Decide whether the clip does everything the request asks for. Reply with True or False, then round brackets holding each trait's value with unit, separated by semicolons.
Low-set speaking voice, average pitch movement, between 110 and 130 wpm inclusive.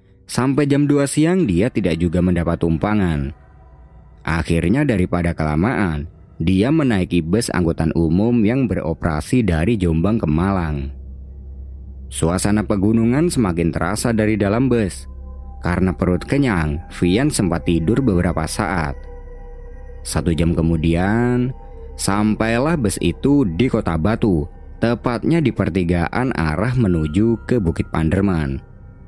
False (90 Hz; 5.9 semitones; 115 wpm)